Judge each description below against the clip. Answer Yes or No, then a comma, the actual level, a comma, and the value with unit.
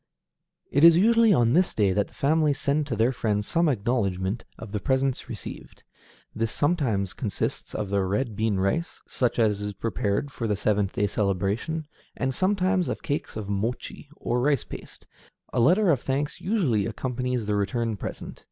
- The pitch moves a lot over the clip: Yes, wide, 6.0 semitones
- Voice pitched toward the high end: No, low, 120 Hz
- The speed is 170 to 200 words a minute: Yes, average, 175 wpm